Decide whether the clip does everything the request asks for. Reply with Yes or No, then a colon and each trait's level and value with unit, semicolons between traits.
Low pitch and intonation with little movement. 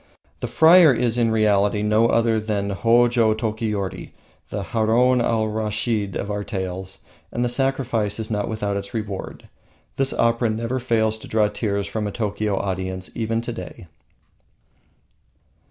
Yes: low, 110 Hz; narrow, 2.3 semitones